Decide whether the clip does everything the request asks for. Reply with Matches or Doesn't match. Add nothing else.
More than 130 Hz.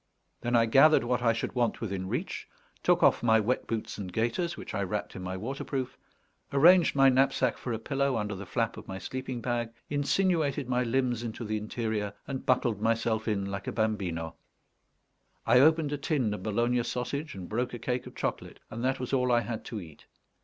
Doesn't match